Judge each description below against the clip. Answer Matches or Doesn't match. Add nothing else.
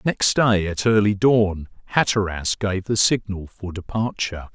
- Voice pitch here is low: Matches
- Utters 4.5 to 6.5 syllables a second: Doesn't match